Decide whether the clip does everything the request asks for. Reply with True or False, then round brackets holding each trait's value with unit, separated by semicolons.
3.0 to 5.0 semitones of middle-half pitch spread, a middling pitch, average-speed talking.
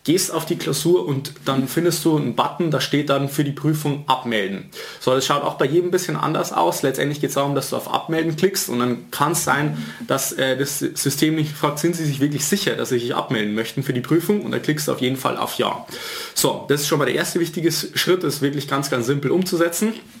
False (3.8 semitones; 145 Hz; 250 wpm)